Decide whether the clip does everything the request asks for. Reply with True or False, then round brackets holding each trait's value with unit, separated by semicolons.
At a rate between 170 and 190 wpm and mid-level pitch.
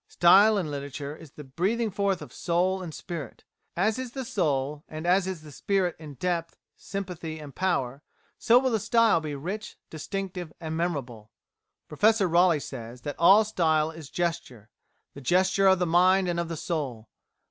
True (175 wpm; 170 Hz)